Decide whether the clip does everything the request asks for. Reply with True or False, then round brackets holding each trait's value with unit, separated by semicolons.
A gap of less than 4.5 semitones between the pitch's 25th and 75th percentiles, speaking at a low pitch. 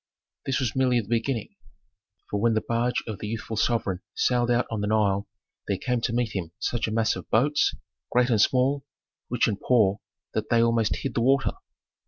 True (2.4 semitones; 115 Hz)